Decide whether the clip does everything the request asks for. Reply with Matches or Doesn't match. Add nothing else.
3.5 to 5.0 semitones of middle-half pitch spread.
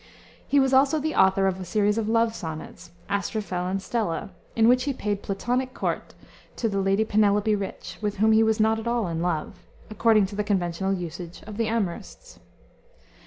Doesn't match